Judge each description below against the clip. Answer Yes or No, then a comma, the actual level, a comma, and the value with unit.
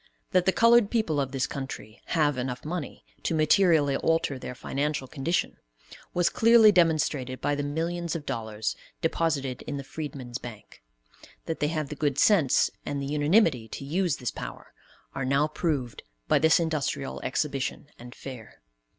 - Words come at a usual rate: Yes, average, 160 wpm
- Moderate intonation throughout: Yes, average, 3.7 semitones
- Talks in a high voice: No, medium, 145 Hz